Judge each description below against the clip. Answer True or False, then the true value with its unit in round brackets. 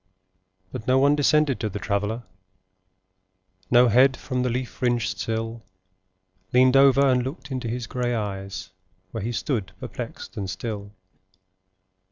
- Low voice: True (120 Hz)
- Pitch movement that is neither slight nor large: True (3.1 semitones)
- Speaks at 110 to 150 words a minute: True (140 wpm)